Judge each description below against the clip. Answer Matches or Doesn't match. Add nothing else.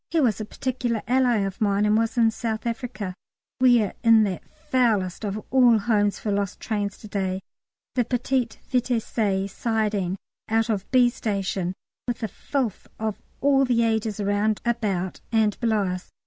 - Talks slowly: Doesn't match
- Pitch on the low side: Doesn't match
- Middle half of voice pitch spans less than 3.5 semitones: Matches